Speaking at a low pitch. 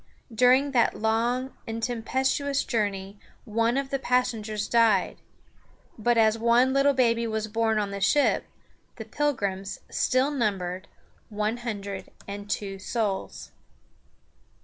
No: high, 230 Hz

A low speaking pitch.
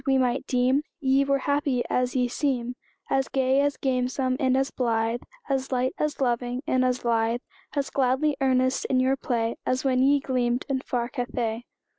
No: very high, 255 Hz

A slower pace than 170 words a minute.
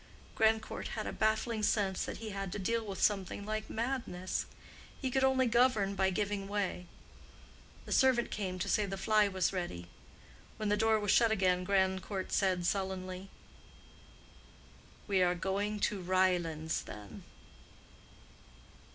Yes: average, 145 wpm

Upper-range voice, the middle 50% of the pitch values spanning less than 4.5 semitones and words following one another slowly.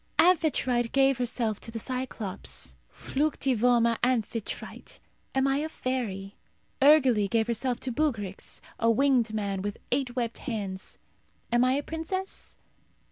Yes: high, 245 Hz; average, 3.5 semitones; slow, 130 wpm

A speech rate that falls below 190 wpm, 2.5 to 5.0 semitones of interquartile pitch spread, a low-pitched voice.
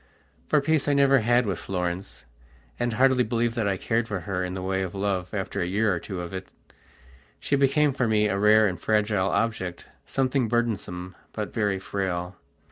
No: average, 195 wpm; average, 4.2 semitones; low, 105 Hz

